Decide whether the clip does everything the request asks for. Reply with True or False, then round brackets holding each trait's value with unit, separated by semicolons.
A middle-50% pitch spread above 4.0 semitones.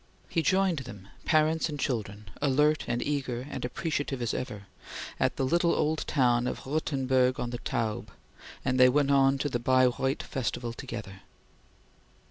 False (3.3 semitones)